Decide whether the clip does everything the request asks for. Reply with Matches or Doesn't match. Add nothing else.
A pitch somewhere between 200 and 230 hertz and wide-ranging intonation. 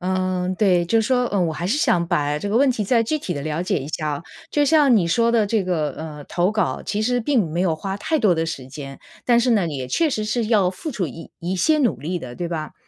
Doesn't match